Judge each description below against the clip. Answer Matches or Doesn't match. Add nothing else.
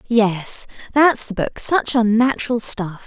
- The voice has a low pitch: Doesn't match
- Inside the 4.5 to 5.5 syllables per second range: Doesn't match